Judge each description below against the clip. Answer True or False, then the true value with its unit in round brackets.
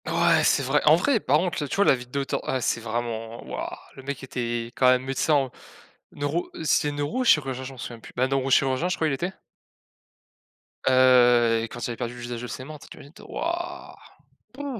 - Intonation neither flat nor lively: True (3.5 semitones)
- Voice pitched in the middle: False (130 Hz)